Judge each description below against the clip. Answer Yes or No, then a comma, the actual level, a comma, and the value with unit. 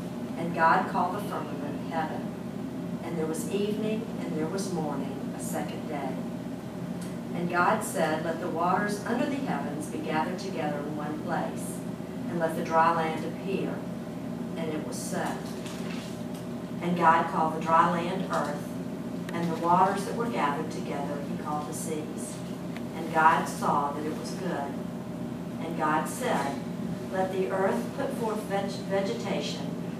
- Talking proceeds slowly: No, average, 155 wpm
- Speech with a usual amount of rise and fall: Yes, average, 3.5 semitones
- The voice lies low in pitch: No, high, 190 Hz